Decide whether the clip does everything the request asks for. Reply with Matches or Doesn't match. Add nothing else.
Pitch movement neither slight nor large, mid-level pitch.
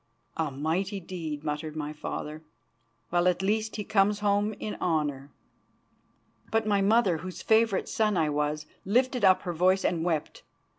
Matches